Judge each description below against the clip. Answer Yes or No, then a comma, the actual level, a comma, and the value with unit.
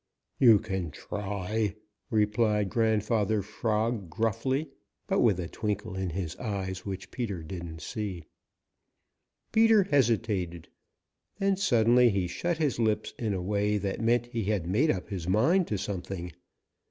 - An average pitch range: Yes, average, 3.6 semitones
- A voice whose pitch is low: Yes, low, 105 Hz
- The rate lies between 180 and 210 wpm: No, average, 140 wpm